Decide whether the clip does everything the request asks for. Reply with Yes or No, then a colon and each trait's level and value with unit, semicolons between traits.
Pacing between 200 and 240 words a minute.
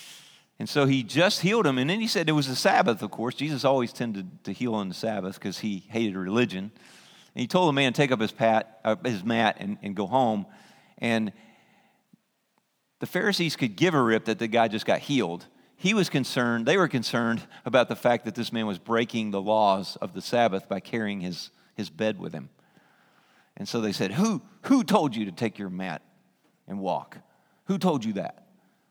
Yes: fast, 205 wpm